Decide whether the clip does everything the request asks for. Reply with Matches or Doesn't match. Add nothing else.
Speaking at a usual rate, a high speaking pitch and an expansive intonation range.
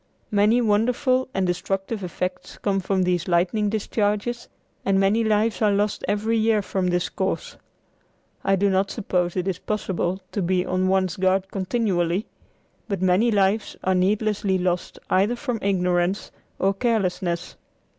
Doesn't match